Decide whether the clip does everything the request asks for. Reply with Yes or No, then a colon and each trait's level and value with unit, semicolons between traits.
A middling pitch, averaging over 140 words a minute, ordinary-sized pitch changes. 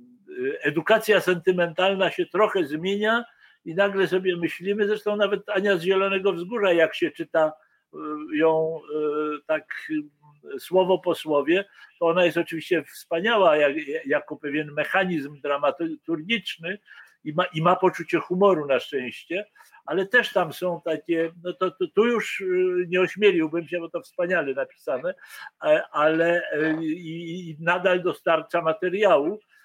No: medium, 180 Hz; average, 120 wpm; average, 3.8 semitones